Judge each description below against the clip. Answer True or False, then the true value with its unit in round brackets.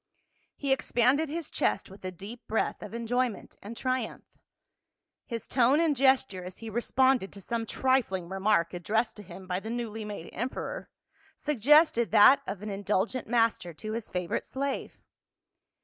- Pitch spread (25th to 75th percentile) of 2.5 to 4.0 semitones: False (4.7 semitones)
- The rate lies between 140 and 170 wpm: True (165 wpm)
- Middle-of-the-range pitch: False (225 Hz)